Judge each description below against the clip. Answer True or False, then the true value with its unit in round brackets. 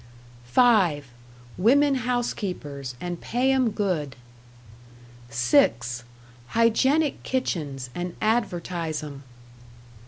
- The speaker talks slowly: True (75 wpm)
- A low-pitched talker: False (180 Hz)